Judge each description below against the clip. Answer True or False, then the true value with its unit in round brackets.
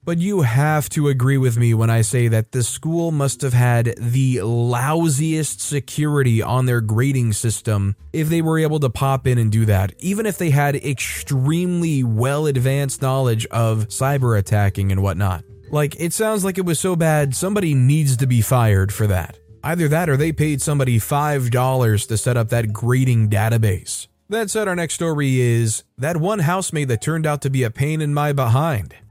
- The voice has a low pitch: True (130 Hz)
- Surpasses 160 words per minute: True (190 wpm)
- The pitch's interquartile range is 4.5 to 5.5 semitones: True (4.8 semitones)